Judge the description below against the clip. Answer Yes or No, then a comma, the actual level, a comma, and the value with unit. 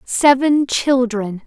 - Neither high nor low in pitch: No, very high, 255 Hz